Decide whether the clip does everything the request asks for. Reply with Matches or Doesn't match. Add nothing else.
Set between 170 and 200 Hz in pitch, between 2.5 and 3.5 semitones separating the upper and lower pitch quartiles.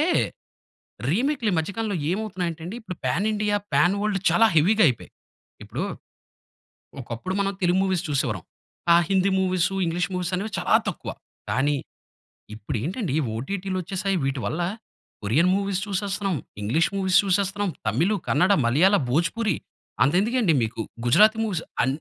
Doesn't match